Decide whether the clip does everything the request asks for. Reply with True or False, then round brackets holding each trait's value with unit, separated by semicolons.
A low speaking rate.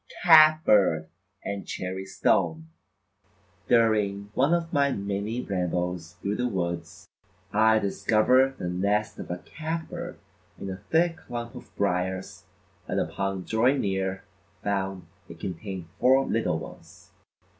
True (130 wpm)